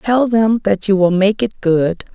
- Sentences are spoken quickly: Yes, fast, 225 wpm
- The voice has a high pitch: Yes, high, 205 Hz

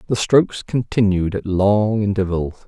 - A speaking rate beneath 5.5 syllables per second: Yes, 4.7 syllables/s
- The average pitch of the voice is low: Yes, low, 100 Hz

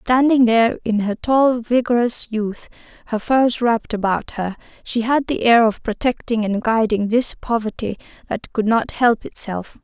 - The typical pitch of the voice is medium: No, high, 230 Hz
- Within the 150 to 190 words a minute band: Yes, average, 165 wpm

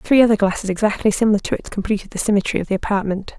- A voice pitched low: No, high, 205 Hz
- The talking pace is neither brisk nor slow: No, fast, 230 wpm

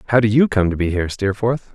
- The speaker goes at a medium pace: No, fast, 275 wpm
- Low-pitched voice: Yes, low, 110 Hz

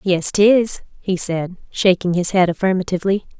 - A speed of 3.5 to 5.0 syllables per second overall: Yes, 4.8 syllables/s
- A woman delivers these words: Yes, female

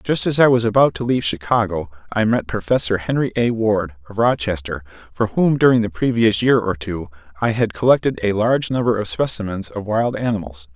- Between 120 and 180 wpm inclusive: No, average, 195 wpm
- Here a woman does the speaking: No, male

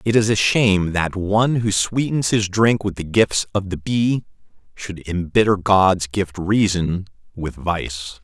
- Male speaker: Yes, male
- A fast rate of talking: No, average, 170 wpm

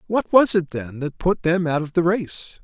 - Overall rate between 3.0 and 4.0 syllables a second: No, 4.8 syllables/s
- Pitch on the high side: No, medium, 170 Hz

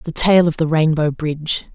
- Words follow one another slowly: No, fast, 205 wpm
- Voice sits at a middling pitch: Yes, medium, 160 Hz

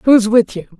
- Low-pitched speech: No, high, 220 Hz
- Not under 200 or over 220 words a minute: No, fast, 230 wpm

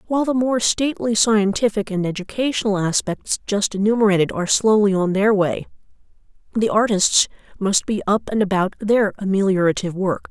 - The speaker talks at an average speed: Yes, average, 145 wpm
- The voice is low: No, high, 205 Hz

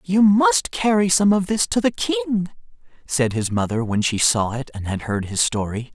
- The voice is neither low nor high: Yes, medium, 150 Hz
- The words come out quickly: Yes, fast, 210 wpm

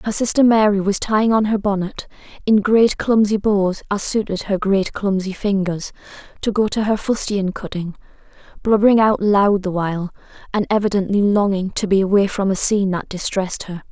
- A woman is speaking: Yes, female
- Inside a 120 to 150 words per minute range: No, average, 175 wpm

